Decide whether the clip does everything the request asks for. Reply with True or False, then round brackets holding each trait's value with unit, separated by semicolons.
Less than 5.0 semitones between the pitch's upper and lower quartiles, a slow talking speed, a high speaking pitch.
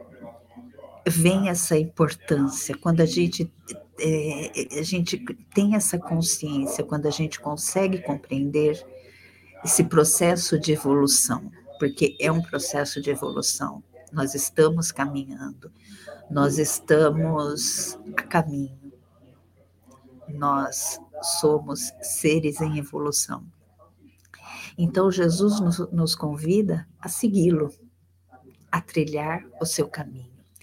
False (3.5 semitones; 100 wpm; 155 Hz)